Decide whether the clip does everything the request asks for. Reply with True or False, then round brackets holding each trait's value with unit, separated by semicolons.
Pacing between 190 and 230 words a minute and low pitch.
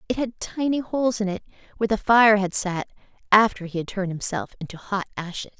False (205 wpm; 205 Hz)